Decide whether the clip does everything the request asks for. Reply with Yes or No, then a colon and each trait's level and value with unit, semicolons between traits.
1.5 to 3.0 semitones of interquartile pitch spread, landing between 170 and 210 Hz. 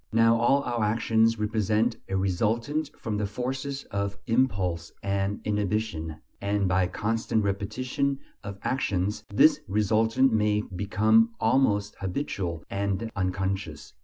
No: average, 2.7 semitones; low, 105 Hz